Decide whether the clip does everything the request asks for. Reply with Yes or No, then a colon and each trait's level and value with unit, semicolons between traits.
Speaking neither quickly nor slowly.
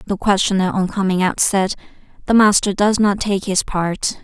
Yes: average, 185 wpm